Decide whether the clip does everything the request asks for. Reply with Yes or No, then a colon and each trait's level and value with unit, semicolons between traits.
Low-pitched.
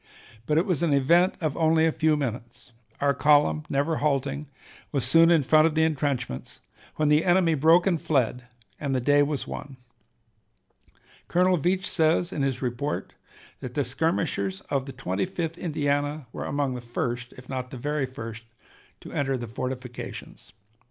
No: medium, 145 Hz